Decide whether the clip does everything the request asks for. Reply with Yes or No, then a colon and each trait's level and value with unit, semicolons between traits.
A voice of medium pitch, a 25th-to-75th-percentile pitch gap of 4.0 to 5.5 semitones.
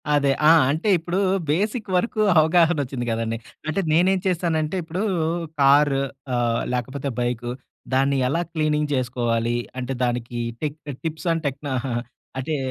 Yes: medium, 145 Hz; average, 4.9 semitones